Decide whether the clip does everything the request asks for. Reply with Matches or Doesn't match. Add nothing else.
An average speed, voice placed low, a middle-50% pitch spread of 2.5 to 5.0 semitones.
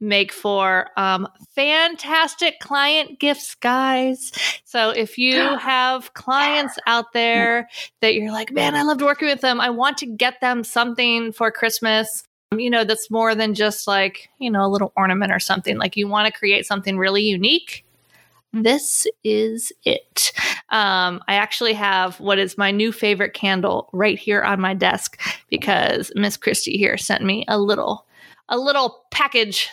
Doesn't match